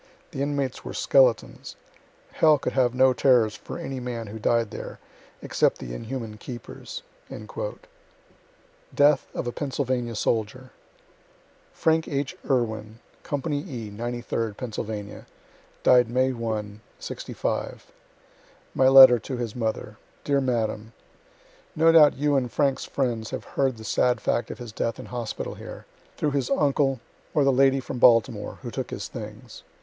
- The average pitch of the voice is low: Yes, low, 125 Hz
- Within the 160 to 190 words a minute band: No, average, 145 wpm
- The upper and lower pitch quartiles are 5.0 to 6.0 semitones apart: No, average, 3.2 semitones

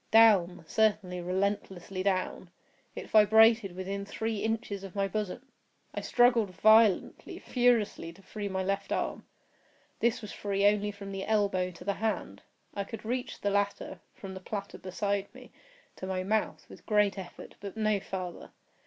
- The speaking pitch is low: No, high, 200 Hz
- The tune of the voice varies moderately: No, narrow, 2.3 semitones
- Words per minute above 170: No, average, 155 wpm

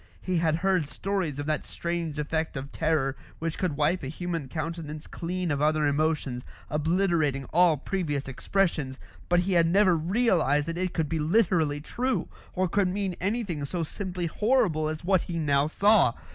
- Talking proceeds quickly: No, average, 175 wpm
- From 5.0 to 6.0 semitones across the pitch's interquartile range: No, average, 3.6 semitones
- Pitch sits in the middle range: Yes, medium, 165 Hz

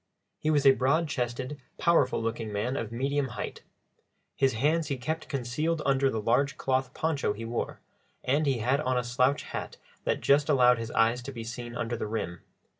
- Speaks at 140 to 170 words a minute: No, average, 190 wpm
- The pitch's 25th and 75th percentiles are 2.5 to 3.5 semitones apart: Yes, average, 3.1 semitones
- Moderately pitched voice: No, low, 130 Hz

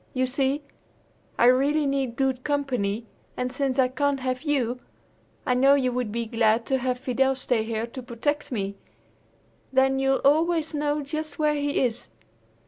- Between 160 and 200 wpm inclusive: Yes, average, 165 wpm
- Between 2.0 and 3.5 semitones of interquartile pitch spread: Yes, narrow, 2.5 semitones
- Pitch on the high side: Yes, very high, 265 Hz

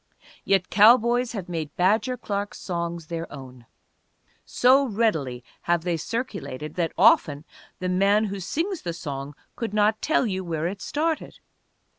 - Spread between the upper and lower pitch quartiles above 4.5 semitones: Yes, wide, 5.4 semitones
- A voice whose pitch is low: No, medium, 185 Hz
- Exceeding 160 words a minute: No, average, 145 wpm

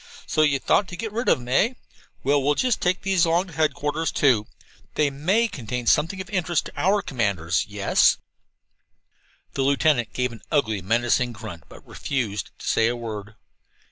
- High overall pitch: No, medium, 140 Hz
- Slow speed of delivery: No, average, 175 wpm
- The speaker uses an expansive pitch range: Yes, wide, 7.1 semitones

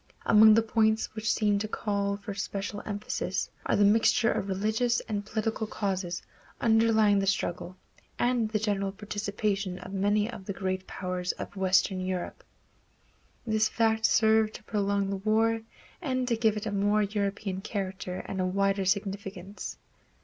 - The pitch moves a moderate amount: No, narrow, 1.9 semitones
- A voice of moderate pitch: No, high, 205 Hz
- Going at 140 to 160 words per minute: Yes, average, 155 wpm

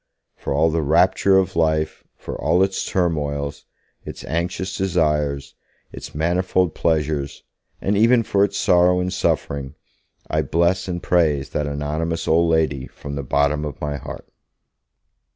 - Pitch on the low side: Yes, very low, 80 Hz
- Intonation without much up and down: No, average, 3.7 semitones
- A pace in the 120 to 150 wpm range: Yes, average, 145 wpm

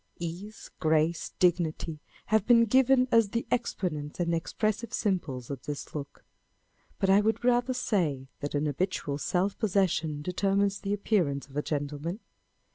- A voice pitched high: No, medium, 180 Hz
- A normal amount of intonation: No, wide, 6.1 semitones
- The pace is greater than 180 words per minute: No, average, 145 wpm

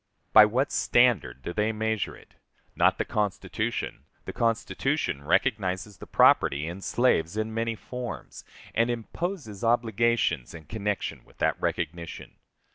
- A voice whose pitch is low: Yes, low, 110 Hz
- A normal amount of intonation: Yes, average, 4.4 semitones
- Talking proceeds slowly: Yes, slow, 130 wpm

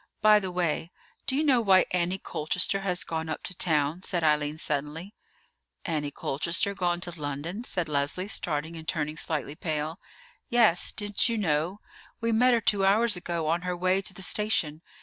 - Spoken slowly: No, average, 180 wpm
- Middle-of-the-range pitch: Yes, medium, 175 Hz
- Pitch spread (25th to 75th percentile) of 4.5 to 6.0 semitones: No, average, 4.1 semitones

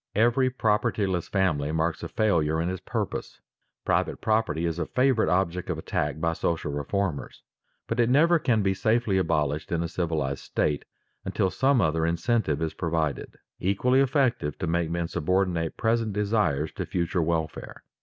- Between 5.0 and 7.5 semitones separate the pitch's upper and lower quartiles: Yes, wide, 5.5 semitones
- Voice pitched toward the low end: Yes, very low, 90 Hz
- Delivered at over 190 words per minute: No, average, 160 wpm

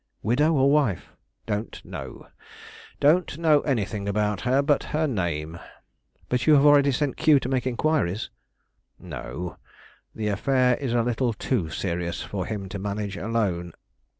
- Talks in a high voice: No, low, 115 Hz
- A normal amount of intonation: No, wide, 5.9 semitones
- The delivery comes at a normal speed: Yes, average, 150 wpm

